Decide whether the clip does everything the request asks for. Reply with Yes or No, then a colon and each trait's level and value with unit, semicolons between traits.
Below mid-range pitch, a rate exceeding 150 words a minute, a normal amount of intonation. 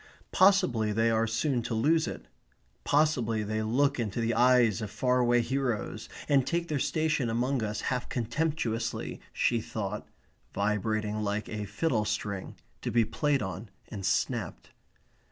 No: low, 115 Hz; average, 145 wpm; average, 3.8 semitones